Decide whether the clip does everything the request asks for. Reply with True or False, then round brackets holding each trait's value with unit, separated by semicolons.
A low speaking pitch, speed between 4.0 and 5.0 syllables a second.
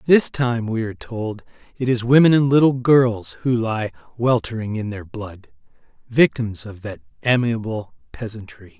True (115 Hz; 4.5 syllables/s)